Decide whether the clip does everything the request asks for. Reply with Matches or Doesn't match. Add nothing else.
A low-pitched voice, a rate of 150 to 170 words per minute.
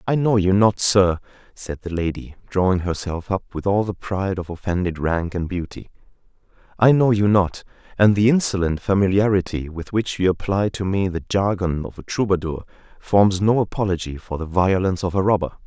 Doesn't match